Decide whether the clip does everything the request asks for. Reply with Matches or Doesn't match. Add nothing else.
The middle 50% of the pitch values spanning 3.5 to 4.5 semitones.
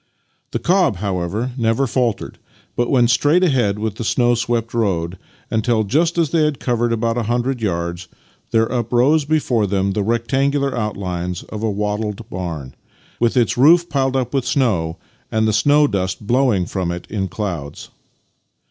Doesn't match